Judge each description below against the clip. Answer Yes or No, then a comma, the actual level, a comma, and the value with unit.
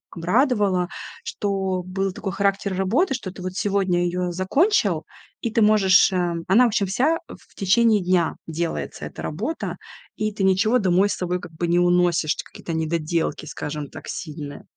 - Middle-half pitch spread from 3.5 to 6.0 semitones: No, average, 3.0 semitones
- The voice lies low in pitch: No, high, 190 Hz